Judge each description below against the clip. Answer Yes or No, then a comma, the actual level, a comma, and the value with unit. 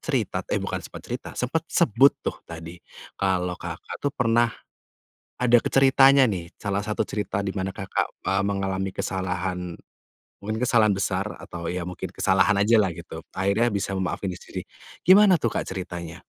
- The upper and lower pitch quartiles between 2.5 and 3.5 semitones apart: No, average, 4.3 semitones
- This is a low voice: Yes, low, 100 Hz